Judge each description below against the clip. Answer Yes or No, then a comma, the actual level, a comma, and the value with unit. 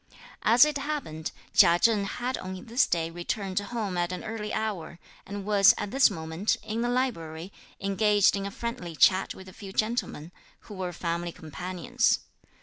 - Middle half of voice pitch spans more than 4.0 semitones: Yes, average, 4.4 semitones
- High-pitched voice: Yes, high, 195 Hz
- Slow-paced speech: No, average, 170 wpm